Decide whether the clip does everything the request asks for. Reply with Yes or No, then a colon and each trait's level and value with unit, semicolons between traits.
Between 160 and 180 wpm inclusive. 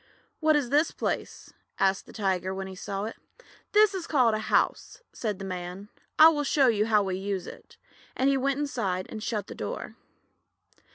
No: average, 190 wpm